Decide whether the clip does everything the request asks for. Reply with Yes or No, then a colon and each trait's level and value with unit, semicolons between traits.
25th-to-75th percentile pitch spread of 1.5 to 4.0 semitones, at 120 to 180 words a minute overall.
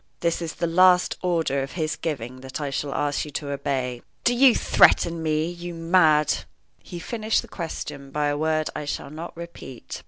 No: average, 3.0 semitones; average, 195 wpm